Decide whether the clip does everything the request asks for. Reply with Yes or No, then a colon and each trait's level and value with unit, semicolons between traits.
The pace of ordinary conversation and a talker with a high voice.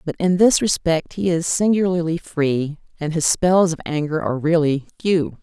No: average, 175 wpm; medium, 165 Hz